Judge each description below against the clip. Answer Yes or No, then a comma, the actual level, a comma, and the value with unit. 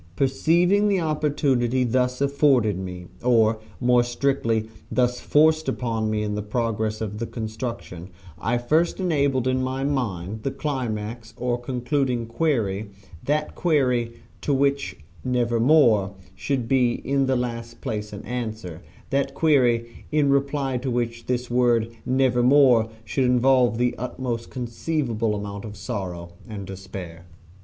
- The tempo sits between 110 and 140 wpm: Yes, slow, 135 wpm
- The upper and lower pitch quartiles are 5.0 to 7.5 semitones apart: No, average, 3.6 semitones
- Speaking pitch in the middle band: No, low, 120 Hz